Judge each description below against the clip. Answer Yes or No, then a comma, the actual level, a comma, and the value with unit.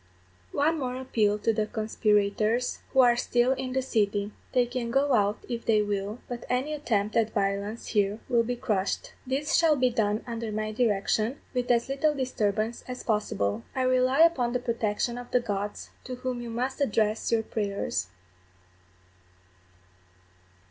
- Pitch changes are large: No, average, 3.3 semitones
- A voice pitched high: Yes, high, 235 Hz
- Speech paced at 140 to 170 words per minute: Yes, average, 160 wpm